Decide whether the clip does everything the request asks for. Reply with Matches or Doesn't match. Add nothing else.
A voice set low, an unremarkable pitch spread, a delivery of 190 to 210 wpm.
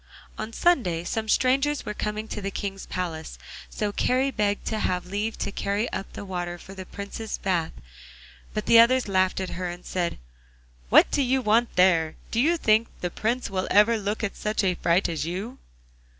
Doesn't match